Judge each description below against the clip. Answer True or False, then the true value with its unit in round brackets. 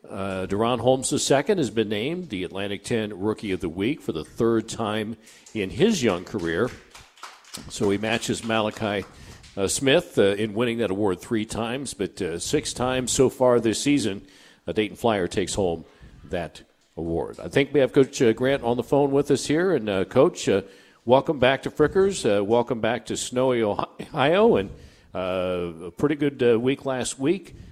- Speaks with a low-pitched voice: True (115 Hz)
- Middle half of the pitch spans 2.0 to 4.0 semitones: False (4.8 semitones)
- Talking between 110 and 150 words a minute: False (190 wpm)